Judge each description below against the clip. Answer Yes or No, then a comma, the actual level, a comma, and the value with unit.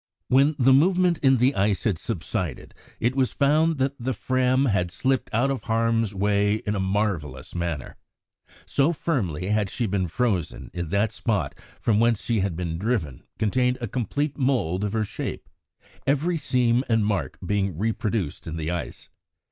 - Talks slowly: No, average, 170 wpm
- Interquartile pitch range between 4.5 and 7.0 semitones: Yes, average, 5.3 semitones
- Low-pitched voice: Yes, low, 110 Hz